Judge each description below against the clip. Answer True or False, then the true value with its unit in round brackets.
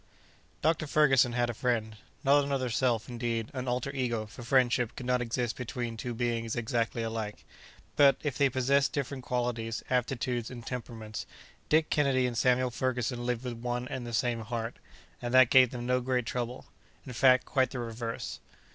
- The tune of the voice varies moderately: False (1.8 semitones)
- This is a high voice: False (125 Hz)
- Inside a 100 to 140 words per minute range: False (175 wpm)